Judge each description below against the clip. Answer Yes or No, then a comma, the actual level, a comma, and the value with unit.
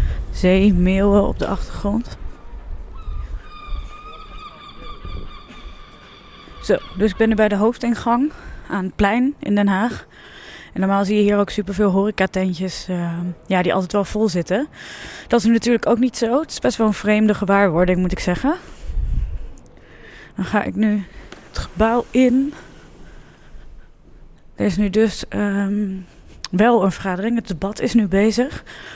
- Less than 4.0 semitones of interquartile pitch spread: Yes, average, 3.6 semitones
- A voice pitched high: Yes, high, 205 Hz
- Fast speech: No, average, 145 wpm